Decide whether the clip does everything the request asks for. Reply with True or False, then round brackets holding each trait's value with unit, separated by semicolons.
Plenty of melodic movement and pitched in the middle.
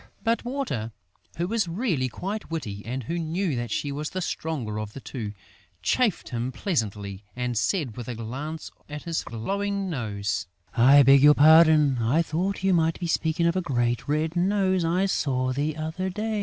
True (6.7 semitones; 155 Hz)